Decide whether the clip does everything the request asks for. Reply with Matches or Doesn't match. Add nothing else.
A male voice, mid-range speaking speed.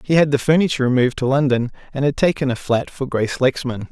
Doesn't match